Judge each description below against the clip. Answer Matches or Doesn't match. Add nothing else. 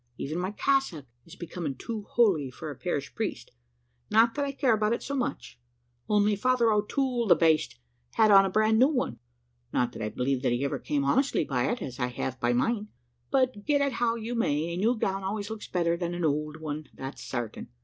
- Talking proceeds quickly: Matches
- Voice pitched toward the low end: Doesn't match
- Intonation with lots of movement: Matches